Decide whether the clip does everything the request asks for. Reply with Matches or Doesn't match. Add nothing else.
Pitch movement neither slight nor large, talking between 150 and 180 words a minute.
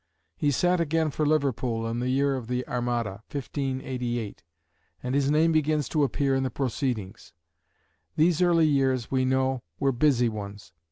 Matches